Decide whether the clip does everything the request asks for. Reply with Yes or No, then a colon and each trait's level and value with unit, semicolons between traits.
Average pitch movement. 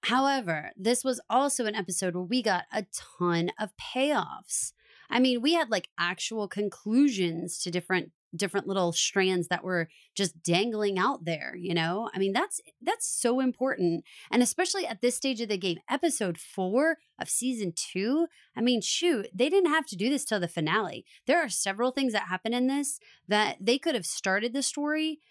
No: wide, 6.4 semitones